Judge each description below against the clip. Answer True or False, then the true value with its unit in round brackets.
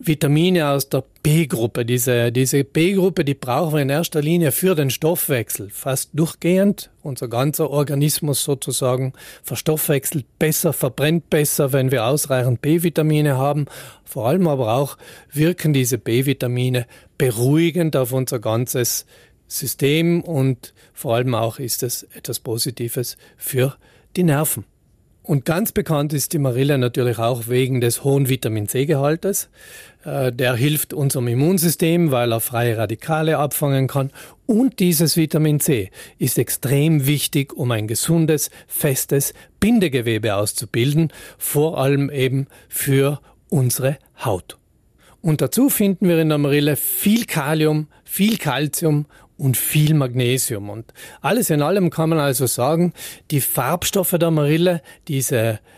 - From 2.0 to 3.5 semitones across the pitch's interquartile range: False (3.9 semitones)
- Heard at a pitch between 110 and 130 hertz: False (140 Hz)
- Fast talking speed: False (130 wpm)